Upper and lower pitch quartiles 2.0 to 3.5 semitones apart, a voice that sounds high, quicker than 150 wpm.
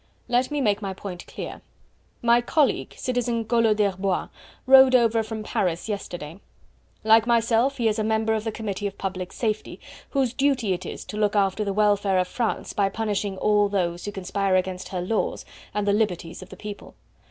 Yes: average, 2.9 semitones; high, 210 Hz; average, 185 wpm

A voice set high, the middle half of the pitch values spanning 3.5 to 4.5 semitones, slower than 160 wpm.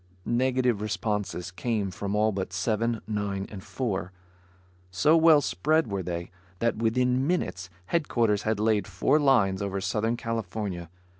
No: low, 105 Hz; average, 3.9 semitones; average, 140 wpm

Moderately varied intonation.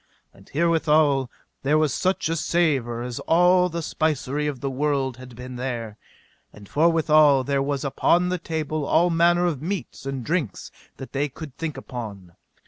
Yes: average, 4.1 semitones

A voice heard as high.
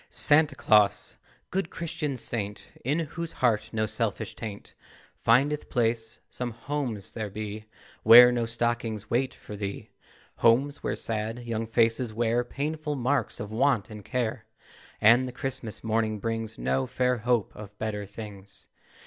No: low, 115 Hz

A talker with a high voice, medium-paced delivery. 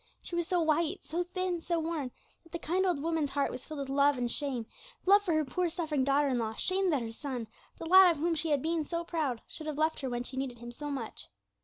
No: very high, 310 Hz; fast, 270 wpm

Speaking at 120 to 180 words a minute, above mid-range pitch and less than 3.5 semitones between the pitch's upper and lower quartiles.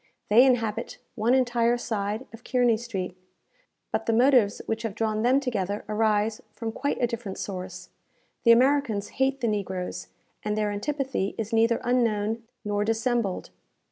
Yes: average, 150 wpm; high, 225 Hz; average, 2.8 semitones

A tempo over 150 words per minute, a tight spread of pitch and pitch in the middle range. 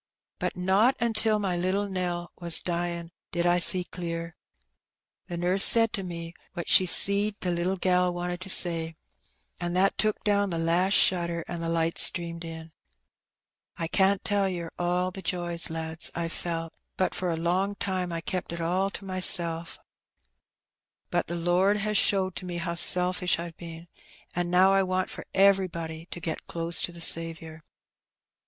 Yes: average, 175 wpm; narrow, 2.1 semitones; medium, 175 Hz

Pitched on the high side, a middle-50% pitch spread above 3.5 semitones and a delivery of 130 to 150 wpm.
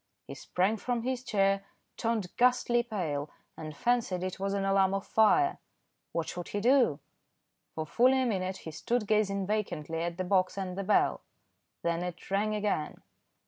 No: high, 195 Hz; average, 4.0 semitones; average, 170 wpm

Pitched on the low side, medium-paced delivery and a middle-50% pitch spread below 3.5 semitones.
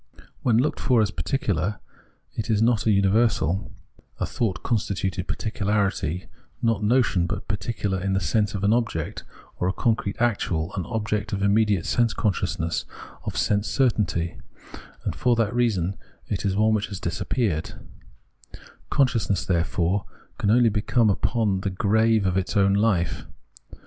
Yes: low, 105 Hz; average, 150 wpm; average, 3.0 semitones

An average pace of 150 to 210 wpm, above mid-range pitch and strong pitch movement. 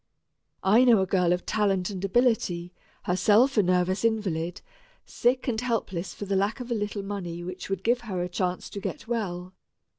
No: average, 185 wpm; high, 195 Hz; average, 3.7 semitones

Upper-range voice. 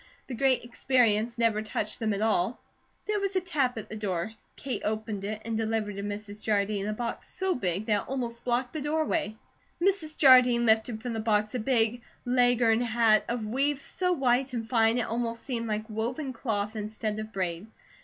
Yes: high, 230 Hz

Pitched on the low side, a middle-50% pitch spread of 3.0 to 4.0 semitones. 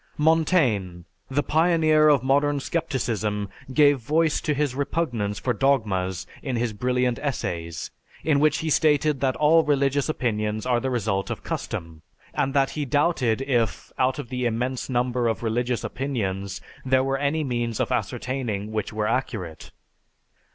No: low, 130 Hz; average, 4.6 semitones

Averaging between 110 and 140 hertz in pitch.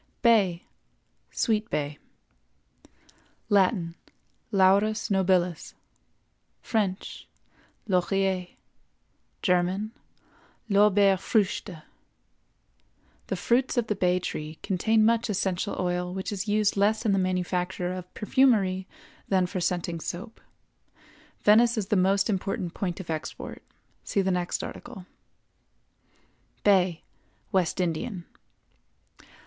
No: high, 190 Hz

